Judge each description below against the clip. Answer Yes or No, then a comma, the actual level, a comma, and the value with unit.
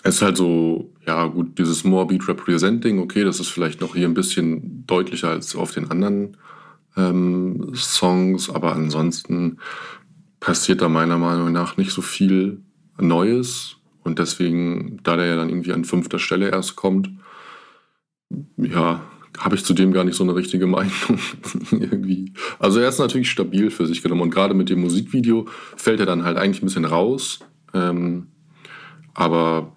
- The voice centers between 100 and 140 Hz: No, very low, 90 Hz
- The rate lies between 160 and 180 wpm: Yes, average, 165 wpm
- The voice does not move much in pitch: Yes, narrow, 2.0 semitones